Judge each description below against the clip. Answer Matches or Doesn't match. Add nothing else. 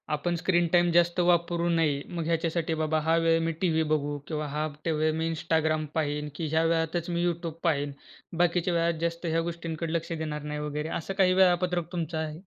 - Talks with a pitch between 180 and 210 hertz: Doesn't match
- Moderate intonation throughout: Doesn't match